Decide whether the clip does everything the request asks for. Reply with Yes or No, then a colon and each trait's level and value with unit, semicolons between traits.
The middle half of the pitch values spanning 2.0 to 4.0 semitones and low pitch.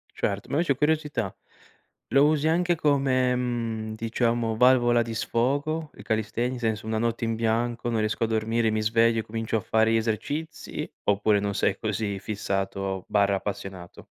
Yes: narrow, 2.6 semitones; low, 115 Hz